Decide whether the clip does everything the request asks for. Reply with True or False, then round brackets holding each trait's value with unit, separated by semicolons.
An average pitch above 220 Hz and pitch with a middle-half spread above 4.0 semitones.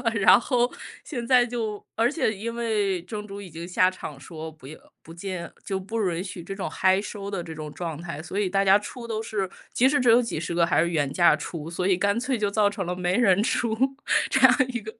False (195 Hz; 4.6 semitones)